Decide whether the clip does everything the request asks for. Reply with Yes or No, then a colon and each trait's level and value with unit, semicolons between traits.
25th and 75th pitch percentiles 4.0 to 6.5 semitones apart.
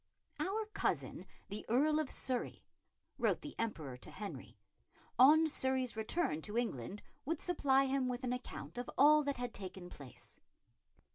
Yes: wide, 5.5 semitones